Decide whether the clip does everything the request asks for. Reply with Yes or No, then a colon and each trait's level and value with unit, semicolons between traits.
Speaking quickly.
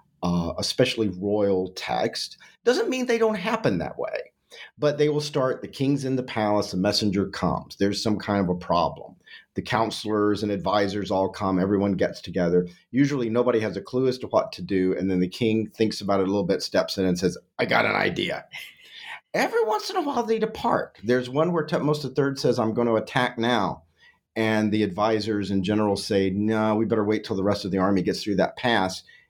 Yes: fast, 215 wpm